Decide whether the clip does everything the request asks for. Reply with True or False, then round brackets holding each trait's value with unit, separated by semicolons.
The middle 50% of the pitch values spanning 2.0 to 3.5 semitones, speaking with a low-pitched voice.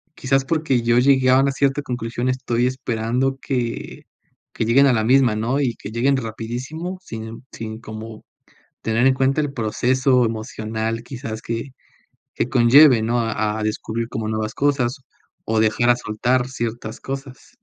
True (2.9 semitones; 120 Hz)